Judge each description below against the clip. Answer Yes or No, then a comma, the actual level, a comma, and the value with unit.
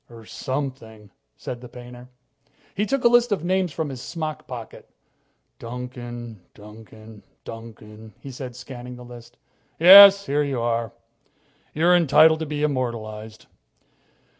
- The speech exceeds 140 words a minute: No, slow, 135 wpm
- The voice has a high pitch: No, low, 125 Hz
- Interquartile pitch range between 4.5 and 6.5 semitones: Yes, average, 5.1 semitones